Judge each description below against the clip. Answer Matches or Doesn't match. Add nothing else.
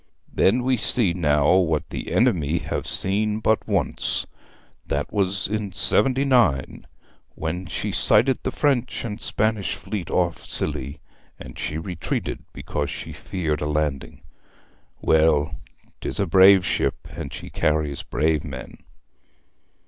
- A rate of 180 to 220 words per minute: Doesn't match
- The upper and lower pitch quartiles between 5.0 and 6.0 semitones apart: Matches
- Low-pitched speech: Matches